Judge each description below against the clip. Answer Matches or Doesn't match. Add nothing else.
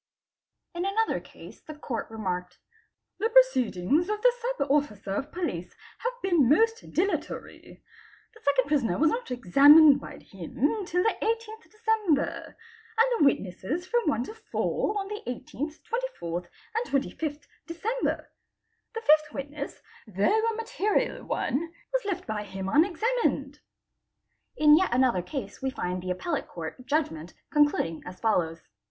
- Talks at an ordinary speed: Matches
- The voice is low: Doesn't match